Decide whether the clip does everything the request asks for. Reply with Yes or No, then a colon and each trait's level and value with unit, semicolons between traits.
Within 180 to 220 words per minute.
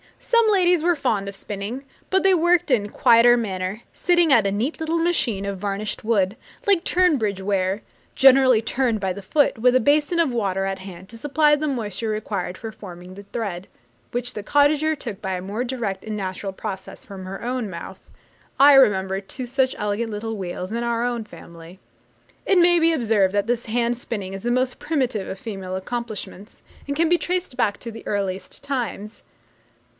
Yes: average, 190 wpm